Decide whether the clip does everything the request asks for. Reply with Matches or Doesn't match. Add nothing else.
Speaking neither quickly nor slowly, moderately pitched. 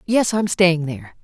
Matches